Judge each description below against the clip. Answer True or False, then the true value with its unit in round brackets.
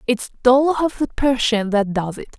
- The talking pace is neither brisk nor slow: True (175 wpm)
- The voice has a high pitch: True (240 Hz)